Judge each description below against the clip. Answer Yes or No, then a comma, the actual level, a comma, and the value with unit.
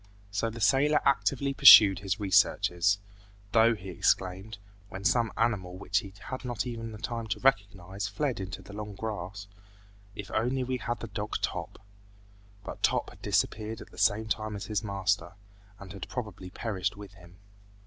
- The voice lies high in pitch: No, low, 105 Hz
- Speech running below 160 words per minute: No, average, 170 wpm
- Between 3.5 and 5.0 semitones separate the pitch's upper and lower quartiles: No, average, 3.0 semitones